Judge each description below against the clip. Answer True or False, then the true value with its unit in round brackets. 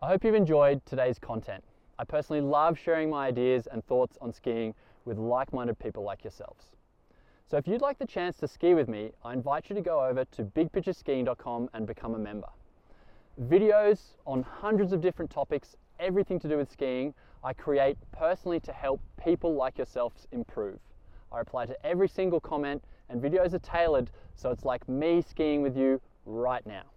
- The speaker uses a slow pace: False (185 wpm)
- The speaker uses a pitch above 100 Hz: True (140 Hz)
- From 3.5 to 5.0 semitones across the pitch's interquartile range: False (5.4 semitones)